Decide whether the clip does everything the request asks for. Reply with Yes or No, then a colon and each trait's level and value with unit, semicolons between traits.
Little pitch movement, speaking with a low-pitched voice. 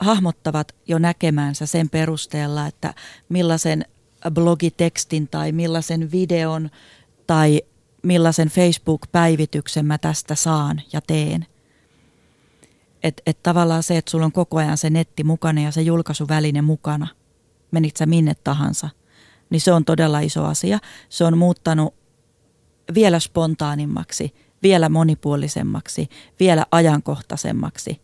No: narrow, 1.8 semitones; medium, 160 Hz